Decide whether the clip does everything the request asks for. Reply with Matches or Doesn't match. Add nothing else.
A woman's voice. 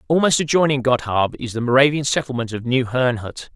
Doesn't match